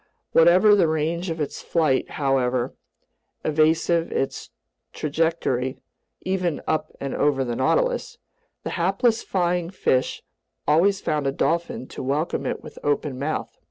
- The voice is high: No, medium, 160 Hz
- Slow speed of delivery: Yes, slow, 130 wpm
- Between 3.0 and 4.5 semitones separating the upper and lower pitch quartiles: Yes, average, 3.9 semitones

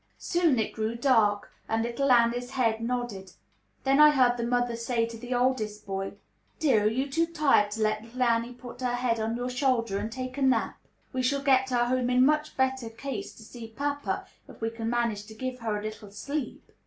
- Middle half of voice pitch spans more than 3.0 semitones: No, narrow, 2.6 semitones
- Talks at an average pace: No, fast, 215 wpm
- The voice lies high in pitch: Yes, high, 245 Hz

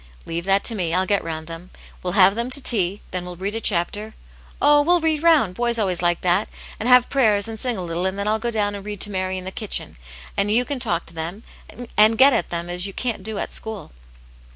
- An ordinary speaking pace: No, fast, 260 wpm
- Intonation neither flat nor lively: Yes, average, 4.1 semitones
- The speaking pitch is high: Yes, high, 200 Hz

